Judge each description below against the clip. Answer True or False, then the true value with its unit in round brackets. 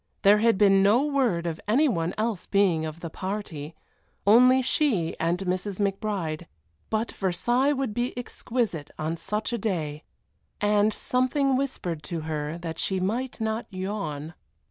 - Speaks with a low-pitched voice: False (200 Hz)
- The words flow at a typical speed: True (150 wpm)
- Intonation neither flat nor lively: False (5.8 semitones)